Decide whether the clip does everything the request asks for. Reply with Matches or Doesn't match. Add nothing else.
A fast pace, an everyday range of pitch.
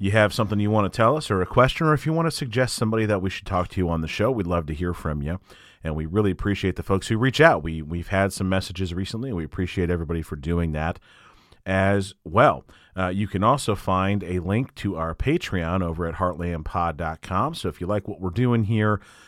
Matches